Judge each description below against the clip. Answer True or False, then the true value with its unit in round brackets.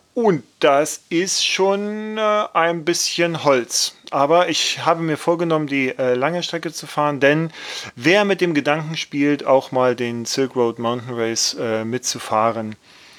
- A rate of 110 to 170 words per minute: True (140 wpm)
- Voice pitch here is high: False (150 Hz)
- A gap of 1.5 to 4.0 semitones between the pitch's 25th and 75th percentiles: False (5.2 semitones)